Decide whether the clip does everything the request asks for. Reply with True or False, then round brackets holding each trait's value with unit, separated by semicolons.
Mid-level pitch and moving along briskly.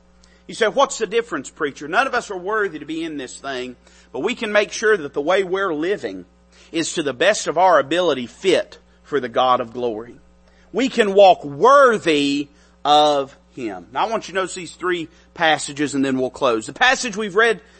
True (165 Hz; 210 wpm)